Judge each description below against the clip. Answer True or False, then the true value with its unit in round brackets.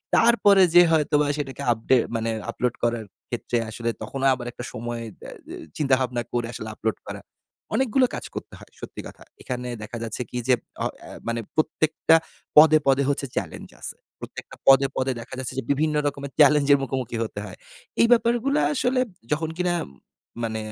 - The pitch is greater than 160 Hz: False (135 Hz)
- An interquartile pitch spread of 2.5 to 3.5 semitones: False (4.8 semitones)